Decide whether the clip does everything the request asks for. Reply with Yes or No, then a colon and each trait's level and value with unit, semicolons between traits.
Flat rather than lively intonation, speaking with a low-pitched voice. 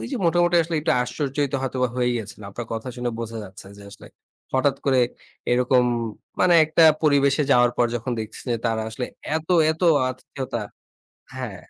No: average, 3.5 semitones; low, 130 Hz